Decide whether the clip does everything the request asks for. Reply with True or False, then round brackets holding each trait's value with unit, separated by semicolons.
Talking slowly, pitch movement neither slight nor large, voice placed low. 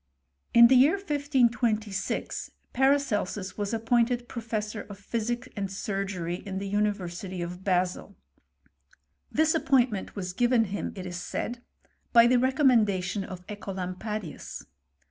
False (125 wpm; 4.1 semitones; 210 Hz)